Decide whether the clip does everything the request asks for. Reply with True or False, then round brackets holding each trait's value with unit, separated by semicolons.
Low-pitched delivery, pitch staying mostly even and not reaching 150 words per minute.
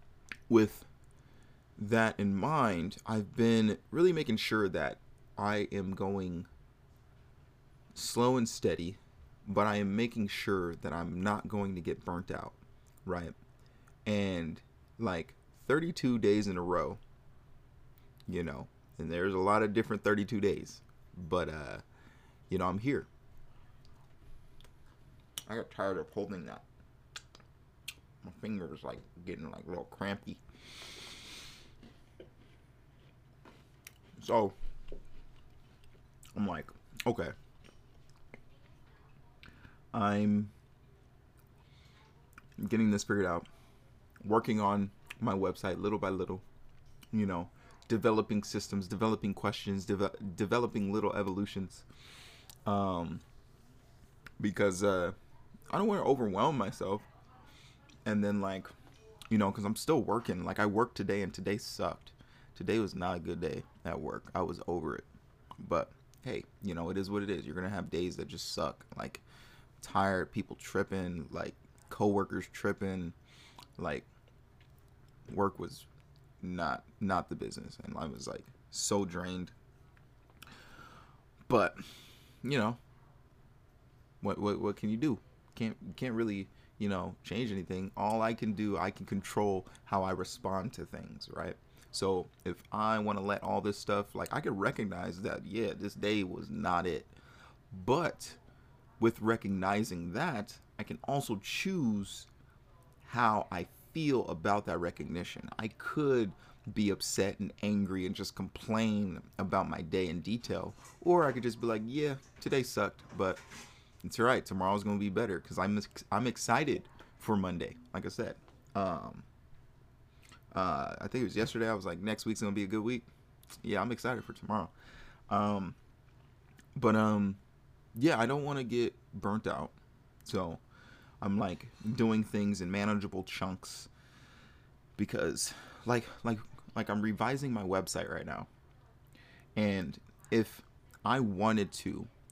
False (105 Hz; 3.7 semitones; 140 wpm)